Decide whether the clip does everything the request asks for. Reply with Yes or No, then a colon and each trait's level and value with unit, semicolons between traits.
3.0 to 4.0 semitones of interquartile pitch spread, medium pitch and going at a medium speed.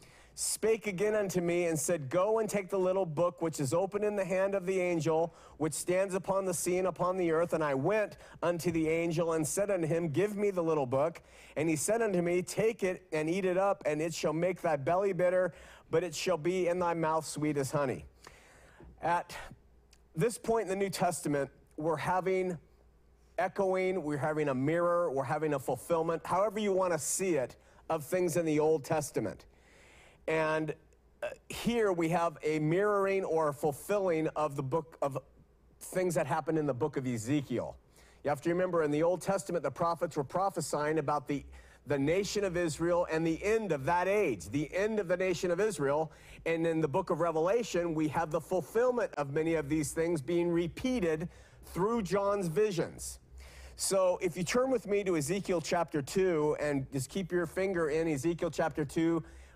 Yes: average, 3.4 semitones; medium, 170 Hz; average, 195 wpm